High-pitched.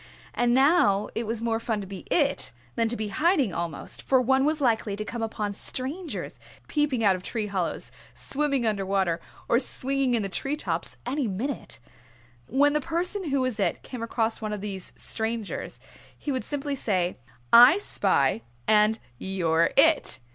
Yes: high, 230 Hz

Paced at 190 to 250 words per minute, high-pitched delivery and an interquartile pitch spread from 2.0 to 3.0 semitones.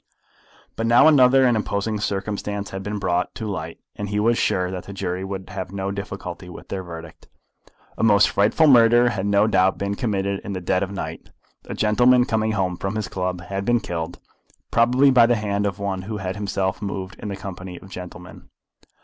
No: fast, 205 wpm; low, 100 Hz; narrow, 2.6 semitones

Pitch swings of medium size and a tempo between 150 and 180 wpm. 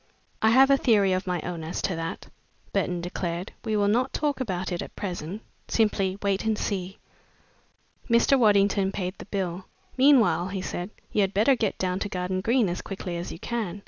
No: average, 3.5 semitones; average, 195 wpm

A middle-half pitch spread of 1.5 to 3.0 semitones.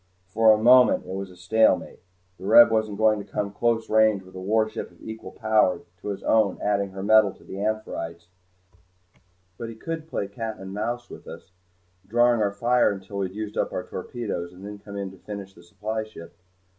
Yes: narrow, 2.4 semitones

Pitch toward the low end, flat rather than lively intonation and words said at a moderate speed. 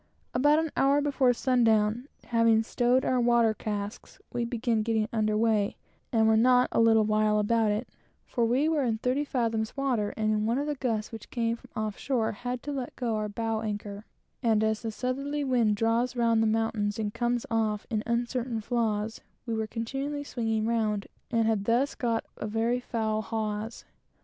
No: high, 230 Hz; narrow, 2.3 semitones; average, 190 wpm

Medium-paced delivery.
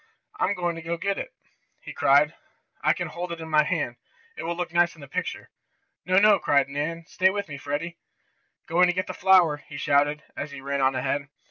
No: fast, 215 wpm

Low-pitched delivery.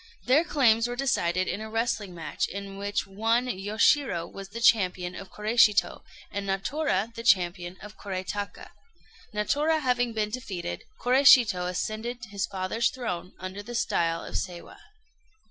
No: high, 210 Hz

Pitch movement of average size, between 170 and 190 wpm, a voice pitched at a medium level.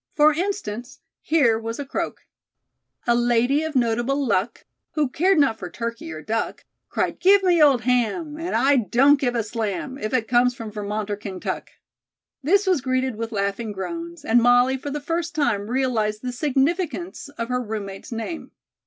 No: average, 4.8 semitones; average, 175 wpm; very high, 250 Hz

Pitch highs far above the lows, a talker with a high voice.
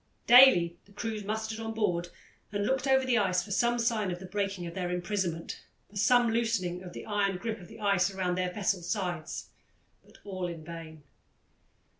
No: average, 3.9 semitones; high, 200 Hz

